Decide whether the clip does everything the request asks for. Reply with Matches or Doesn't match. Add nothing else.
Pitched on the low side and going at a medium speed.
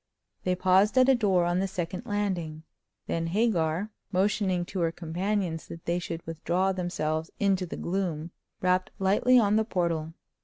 Doesn't match